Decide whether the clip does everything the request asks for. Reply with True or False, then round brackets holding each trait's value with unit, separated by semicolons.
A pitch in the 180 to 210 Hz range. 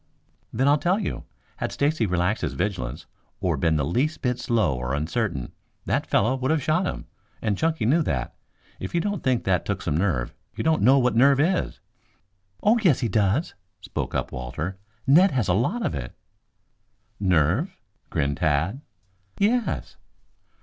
False (110 Hz)